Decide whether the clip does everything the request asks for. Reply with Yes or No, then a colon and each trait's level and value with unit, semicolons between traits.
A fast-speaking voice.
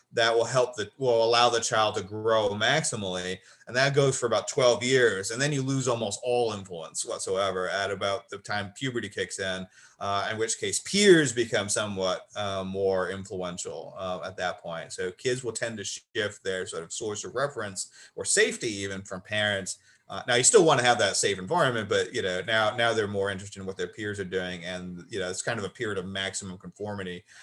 Yes: fast, 215 wpm